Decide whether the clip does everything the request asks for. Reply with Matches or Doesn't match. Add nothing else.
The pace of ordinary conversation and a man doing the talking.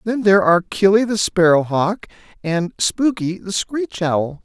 Matches